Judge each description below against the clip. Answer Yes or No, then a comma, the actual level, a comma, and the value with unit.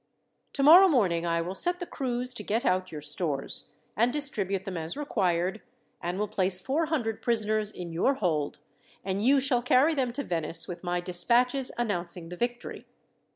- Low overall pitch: No, high, 210 Hz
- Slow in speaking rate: No, average, 175 wpm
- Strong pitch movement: Yes, wide, 6.2 semitones